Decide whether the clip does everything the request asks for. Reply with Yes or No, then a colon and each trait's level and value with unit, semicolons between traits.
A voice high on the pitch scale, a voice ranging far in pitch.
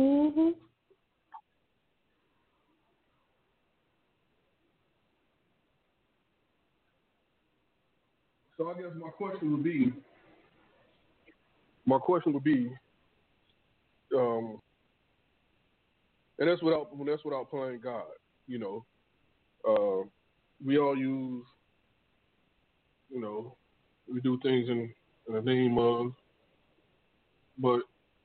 No: low, 135 Hz; wide, 6.3 semitones